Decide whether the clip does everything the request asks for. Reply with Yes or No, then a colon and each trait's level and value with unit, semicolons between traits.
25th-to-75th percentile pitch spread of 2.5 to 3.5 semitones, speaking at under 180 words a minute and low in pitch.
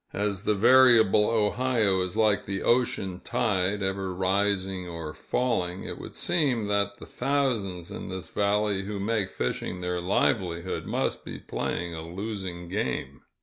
Yes: average, 2.9 semitones; average, 150 wpm; low, 100 Hz